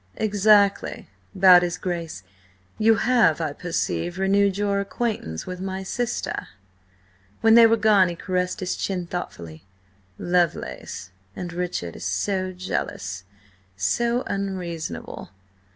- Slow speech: Yes, slow, 120 wpm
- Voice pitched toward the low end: No, medium, 185 Hz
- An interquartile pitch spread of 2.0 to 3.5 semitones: Yes, average, 2.8 semitones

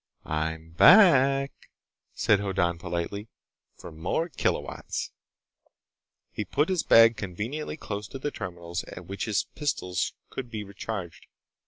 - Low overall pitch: Yes, low, 100 Hz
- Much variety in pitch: Yes, wide, 7.5 semitones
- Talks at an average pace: No, slow, 125 wpm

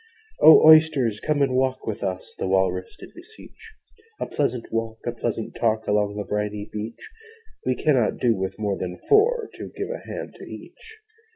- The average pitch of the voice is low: Yes, low, 115 Hz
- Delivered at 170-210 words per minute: Yes, average, 180 wpm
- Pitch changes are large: Yes, wide, 6.1 semitones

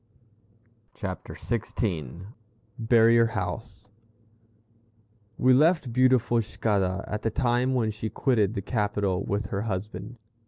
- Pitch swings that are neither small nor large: Yes, average, 3.3 semitones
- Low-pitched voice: Yes, low, 110 Hz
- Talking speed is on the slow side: Yes, slow, 110 wpm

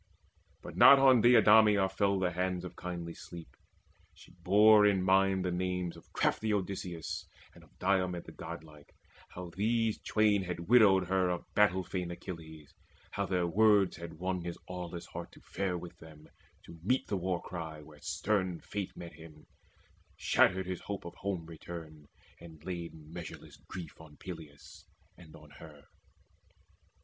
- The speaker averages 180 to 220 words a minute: No, average, 160 wpm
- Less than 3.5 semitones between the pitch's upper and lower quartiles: Yes, narrow, 2.6 semitones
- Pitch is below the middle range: Yes, very low, 90 Hz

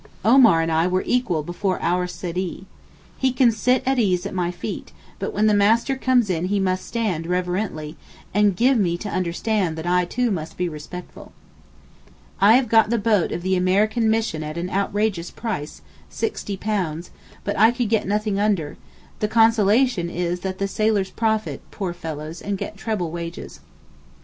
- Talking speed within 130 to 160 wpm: No, average, 175 wpm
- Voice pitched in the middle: No, high, 195 Hz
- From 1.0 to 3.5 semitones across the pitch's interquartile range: No, average, 4.0 semitones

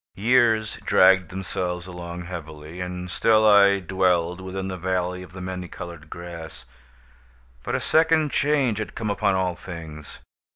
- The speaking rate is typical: Yes, average, 150 wpm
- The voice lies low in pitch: Yes, very low, 90 Hz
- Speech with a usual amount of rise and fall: No, narrow, 2.3 semitones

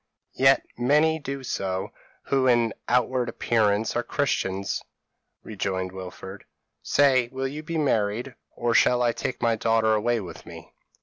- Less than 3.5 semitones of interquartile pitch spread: No, average, 4.2 semitones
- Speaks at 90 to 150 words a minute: Yes, average, 145 wpm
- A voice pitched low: Yes, low, 120 Hz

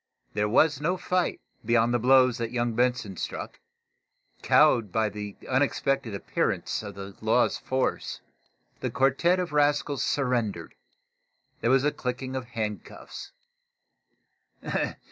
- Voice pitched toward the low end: Yes, low, 125 Hz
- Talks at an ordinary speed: No, slow, 125 wpm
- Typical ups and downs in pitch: Yes, average, 3.8 semitones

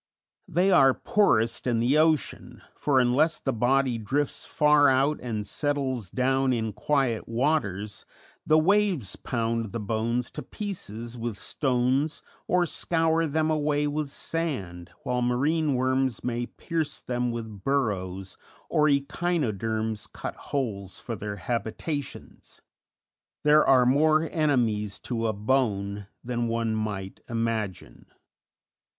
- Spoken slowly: Yes, slow, 125 wpm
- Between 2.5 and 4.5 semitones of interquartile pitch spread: No, average, 4.9 semitones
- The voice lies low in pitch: Yes, low, 125 Hz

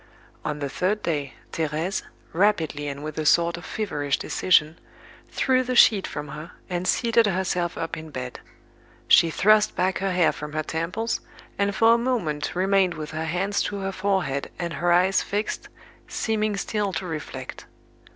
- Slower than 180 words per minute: Yes, average, 170 wpm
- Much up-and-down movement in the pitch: No, average, 4.5 semitones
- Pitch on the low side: No, medium, 180 Hz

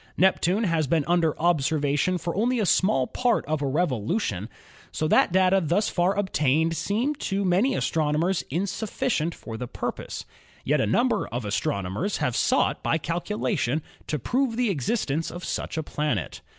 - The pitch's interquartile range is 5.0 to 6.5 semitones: Yes, average, 5.3 semitones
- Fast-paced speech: No, average, 175 wpm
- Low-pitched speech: No, medium, 165 Hz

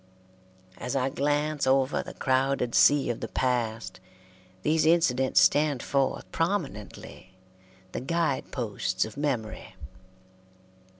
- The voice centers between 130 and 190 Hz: Yes, low, 135 Hz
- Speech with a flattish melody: No, average, 3.5 semitones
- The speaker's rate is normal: No, slow, 110 wpm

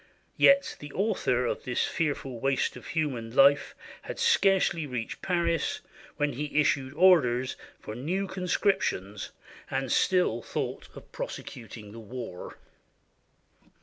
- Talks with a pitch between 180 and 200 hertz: No, medium, 140 Hz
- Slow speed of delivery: Yes, slow, 120 wpm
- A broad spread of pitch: Yes, wide, 6.6 semitones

